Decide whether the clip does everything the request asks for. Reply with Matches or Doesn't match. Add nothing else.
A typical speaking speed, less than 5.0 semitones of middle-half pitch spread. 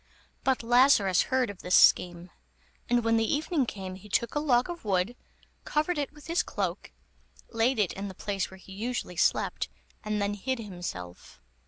Doesn't match